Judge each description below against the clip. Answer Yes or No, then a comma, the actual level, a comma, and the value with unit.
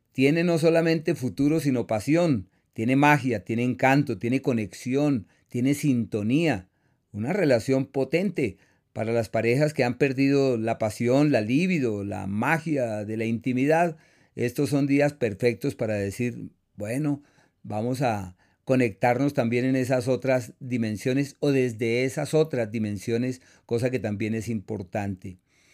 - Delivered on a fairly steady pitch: No, average, 4.0 semitones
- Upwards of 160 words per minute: No, average, 135 wpm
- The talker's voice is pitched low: Yes, low, 125 Hz